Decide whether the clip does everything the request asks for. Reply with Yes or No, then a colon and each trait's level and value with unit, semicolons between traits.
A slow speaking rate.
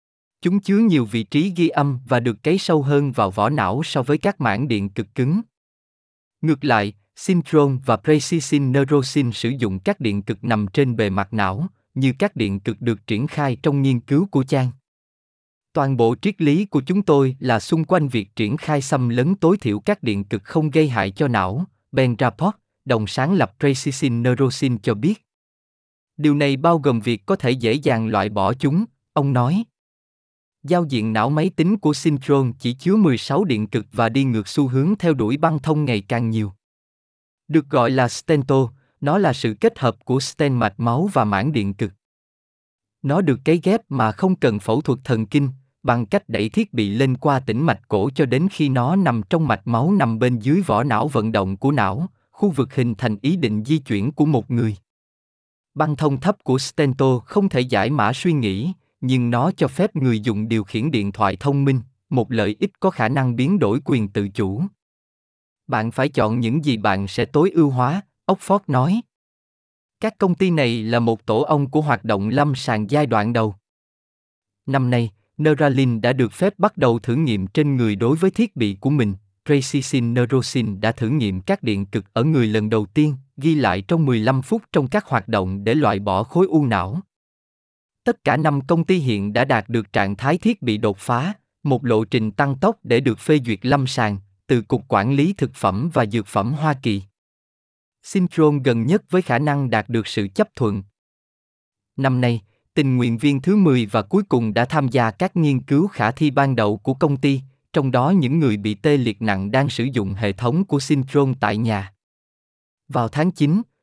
No: average, 205 wpm